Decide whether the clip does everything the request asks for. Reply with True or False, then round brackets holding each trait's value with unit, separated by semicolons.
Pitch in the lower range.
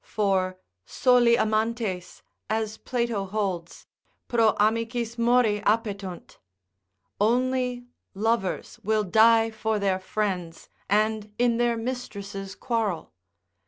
False (220 Hz)